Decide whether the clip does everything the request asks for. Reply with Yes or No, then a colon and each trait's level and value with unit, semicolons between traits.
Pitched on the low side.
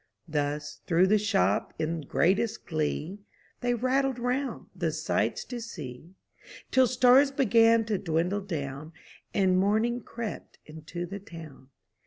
No: high, 195 Hz